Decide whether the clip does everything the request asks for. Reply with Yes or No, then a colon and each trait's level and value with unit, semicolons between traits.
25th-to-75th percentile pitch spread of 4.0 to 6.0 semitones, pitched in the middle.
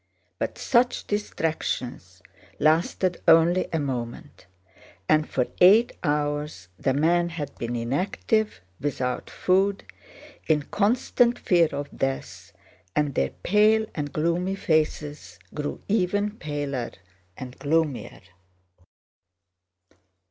Yes: average, 4.9 semitones; medium, 155 Hz